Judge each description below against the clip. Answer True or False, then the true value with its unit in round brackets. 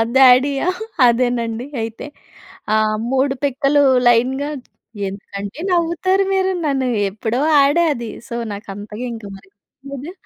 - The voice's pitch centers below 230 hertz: False (255 Hz)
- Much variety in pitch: False (4.0 semitones)